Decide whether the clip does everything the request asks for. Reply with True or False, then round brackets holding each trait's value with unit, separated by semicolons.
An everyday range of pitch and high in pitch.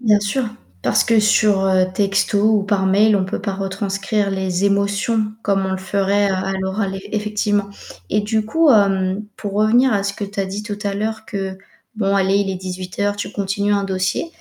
False (1.6 semitones; 200 Hz)